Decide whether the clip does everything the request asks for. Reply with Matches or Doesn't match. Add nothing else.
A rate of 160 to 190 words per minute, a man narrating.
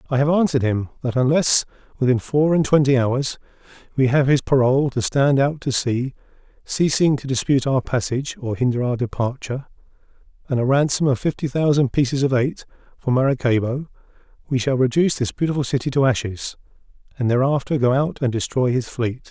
Matches